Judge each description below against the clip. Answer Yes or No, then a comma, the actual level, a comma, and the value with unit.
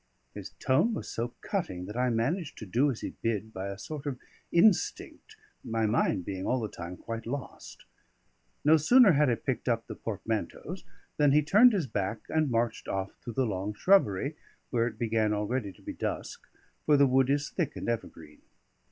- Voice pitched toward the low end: Yes, low, 120 Hz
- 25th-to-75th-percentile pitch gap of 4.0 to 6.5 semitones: Yes, wide, 5.5 semitones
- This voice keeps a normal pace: Yes, average, 190 wpm